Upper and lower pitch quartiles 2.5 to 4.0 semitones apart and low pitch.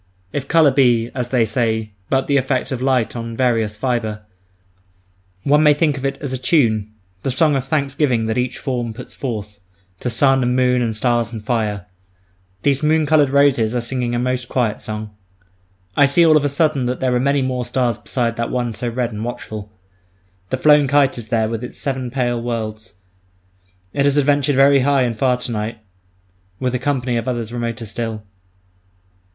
Yes: average, 2.9 semitones; low, 125 Hz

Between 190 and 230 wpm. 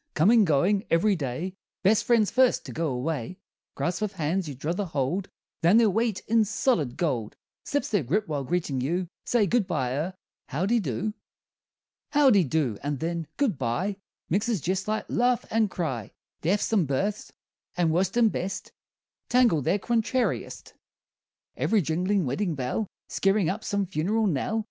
No: average, 160 wpm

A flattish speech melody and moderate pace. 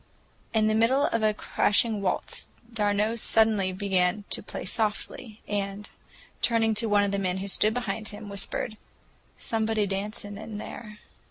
Yes: narrow, 1.7 semitones; average, 155 wpm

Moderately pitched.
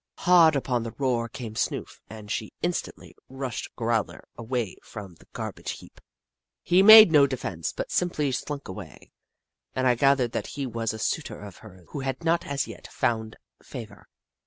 No: low, 125 Hz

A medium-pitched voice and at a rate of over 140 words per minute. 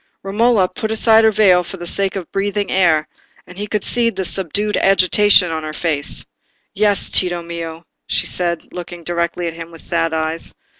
Yes: medium, 180 Hz; average, 190 wpm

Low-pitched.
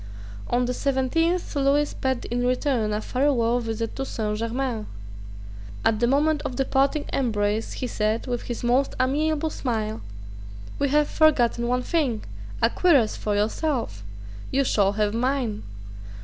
No: very high, 250 Hz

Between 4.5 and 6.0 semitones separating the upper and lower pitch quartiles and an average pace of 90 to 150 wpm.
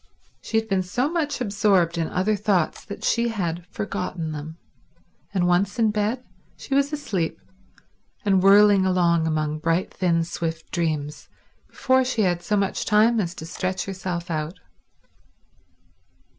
No: average, 4.0 semitones; average, 145 wpm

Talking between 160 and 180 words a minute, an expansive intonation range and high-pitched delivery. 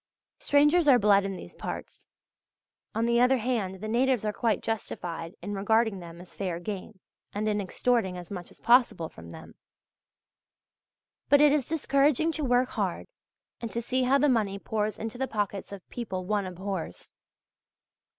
No: average, 170 wpm; average, 4.5 semitones; high, 215 Hz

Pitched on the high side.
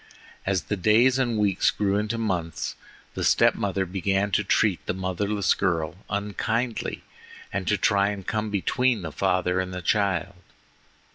No: low, 100 Hz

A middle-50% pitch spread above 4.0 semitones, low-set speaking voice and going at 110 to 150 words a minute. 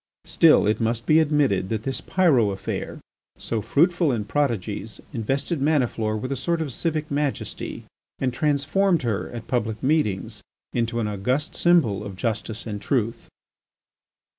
Yes: wide, 5.4 semitones; low, 125 Hz; average, 145 wpm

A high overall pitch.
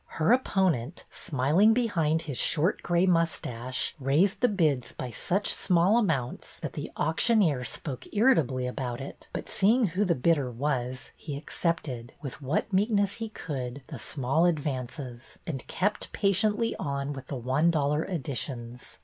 No: medium, 155 Hz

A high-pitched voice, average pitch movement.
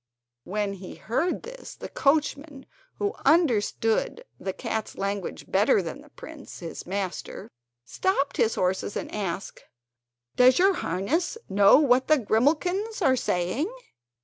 No: very high, 250 Hz; wide, 8.0 semitones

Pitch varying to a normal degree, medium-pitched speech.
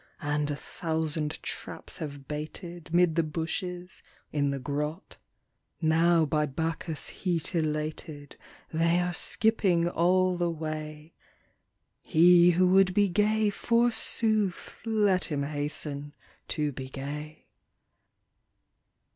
Yes: average, 3.0 semitones; medium, 160 Hz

